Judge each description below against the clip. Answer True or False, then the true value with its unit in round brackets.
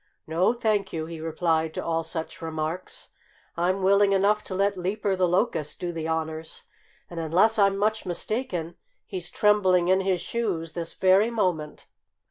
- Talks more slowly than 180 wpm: True (160 wpm)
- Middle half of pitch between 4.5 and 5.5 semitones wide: False (3.5 semitones)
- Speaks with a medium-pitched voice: True (180 Hz)